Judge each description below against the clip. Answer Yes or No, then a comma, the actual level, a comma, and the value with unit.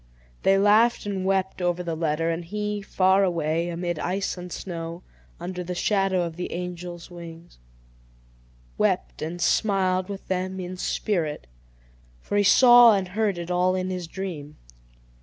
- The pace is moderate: Yes, average, 155 wpm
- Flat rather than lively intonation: Yes, narrow, 2.2 semitones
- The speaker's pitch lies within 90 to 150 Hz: No, medium, 180 Hz